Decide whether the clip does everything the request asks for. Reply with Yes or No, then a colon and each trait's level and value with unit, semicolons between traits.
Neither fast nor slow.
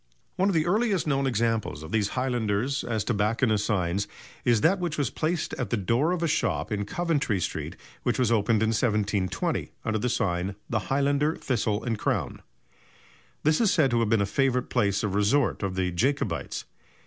Yes: average, 190 wpm